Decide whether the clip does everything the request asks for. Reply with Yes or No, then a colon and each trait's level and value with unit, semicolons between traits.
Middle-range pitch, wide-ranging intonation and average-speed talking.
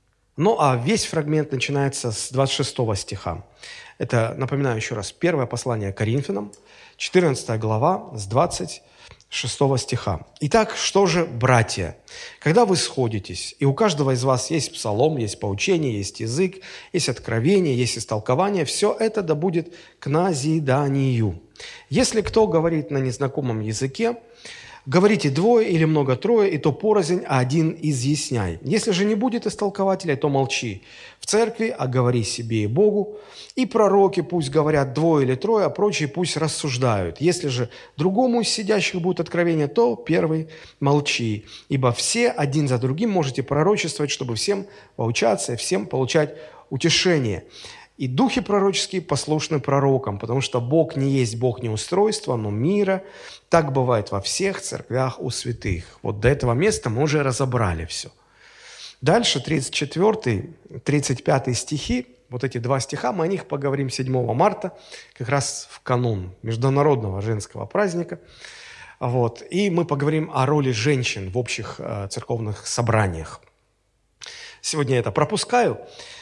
Yes: medium, 145 Hz; wide, 6.7 semitones; average, 140 wpm